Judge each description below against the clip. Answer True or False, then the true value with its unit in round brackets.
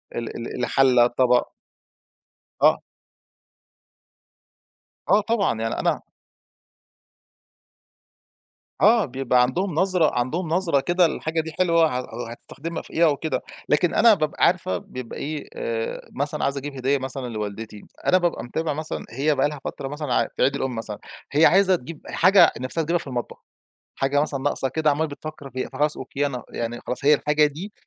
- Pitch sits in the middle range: True (145 Hz)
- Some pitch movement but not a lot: True (4.6 semitones)